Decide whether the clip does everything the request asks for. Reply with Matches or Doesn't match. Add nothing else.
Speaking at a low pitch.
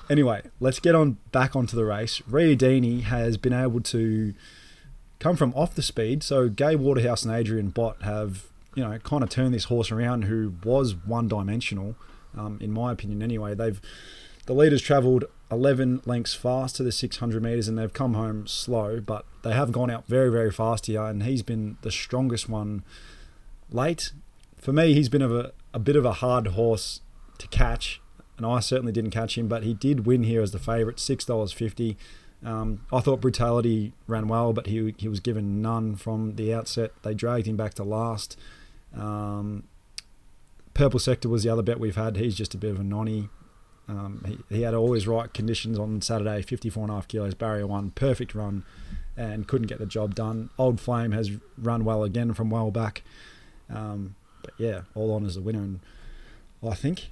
Matches